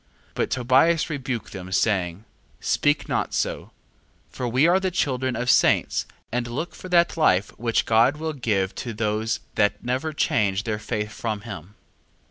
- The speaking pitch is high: No, low, 120 Hz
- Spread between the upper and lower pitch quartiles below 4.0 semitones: No, average, 5.2 semitones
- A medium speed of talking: Yes, average, 170 wpm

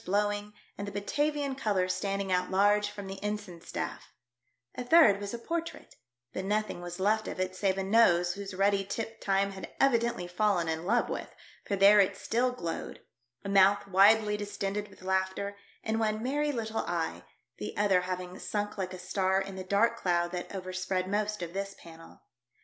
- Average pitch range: No, narrow, 2.2 semitones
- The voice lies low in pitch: No, high, 200 Hz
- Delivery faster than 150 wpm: Yes, average, 185 wpm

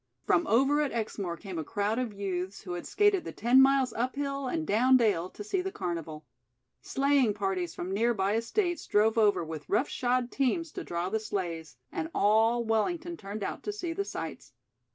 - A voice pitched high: Yes, high, 220 Hz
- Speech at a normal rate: Yes, average, 195 wpm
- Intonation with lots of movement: Yes, wide, 6.1 semitones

